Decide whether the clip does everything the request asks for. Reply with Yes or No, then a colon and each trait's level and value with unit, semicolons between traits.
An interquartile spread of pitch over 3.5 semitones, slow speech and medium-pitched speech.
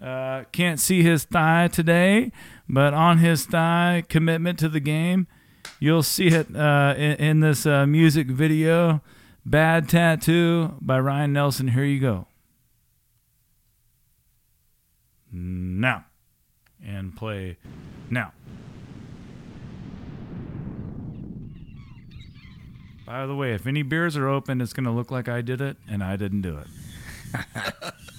Yes: average, 4.5 semitones; slow, 120 wpm; medium, 145 Hz